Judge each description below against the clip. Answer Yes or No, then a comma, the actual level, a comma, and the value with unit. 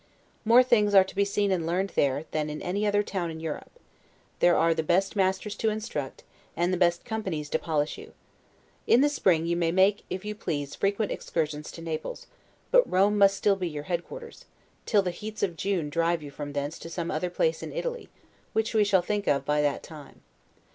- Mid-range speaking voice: Yes, medium, 180 Hz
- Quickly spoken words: Yes, fast, 210 wpm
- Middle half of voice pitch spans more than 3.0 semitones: Yes, average, 4.3 semitones